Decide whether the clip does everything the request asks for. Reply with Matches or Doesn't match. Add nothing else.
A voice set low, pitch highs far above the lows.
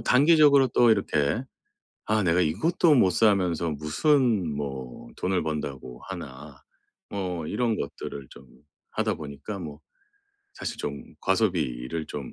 Matches